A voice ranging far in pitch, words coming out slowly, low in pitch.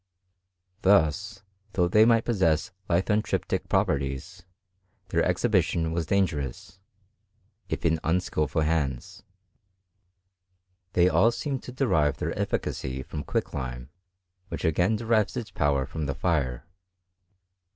Yes: wide, 5.7 semitones; slow, 115 wpm; very low, 80 Hz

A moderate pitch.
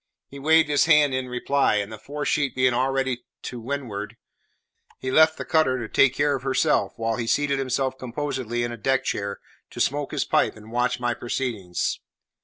No: low, 130 Hz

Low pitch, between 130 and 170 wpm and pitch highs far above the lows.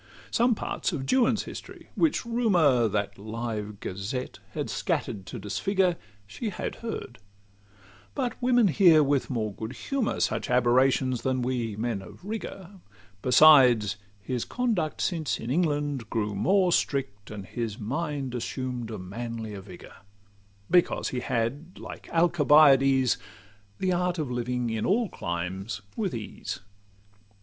Yes: low, 130 Hz; slow, 135 wpm; wide, 7.7 semitones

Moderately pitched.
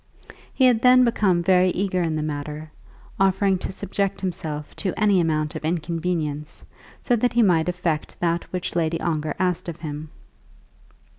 Yes: medium, 175 Hz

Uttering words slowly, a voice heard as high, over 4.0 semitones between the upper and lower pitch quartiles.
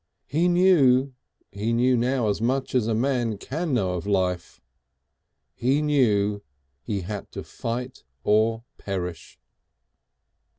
No: slow, 125 wpm; low, 115 Hz; average, 4.4 semitones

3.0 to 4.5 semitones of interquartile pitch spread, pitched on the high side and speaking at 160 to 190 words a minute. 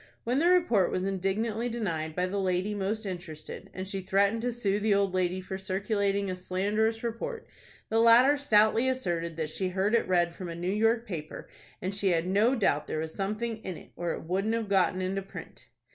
No: average, 3.4 semitones; high, 195 Hz; fast, 205 wpm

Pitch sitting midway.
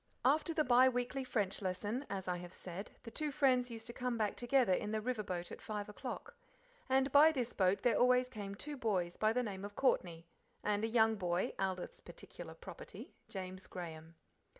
No: high, 220 Hz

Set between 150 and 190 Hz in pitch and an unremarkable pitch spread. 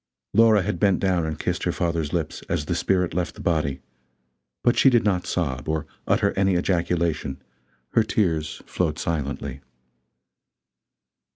No: very low, 85 Hz; average, 3.7 semitones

